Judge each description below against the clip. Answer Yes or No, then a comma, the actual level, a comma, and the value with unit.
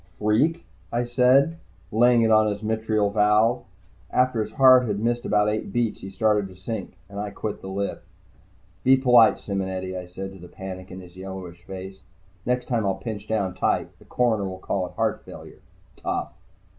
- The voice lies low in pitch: Yes, low, 105 Hz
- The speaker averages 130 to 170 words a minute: No, average, 185 wpm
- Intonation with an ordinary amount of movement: Yes, average, 3.7 semitones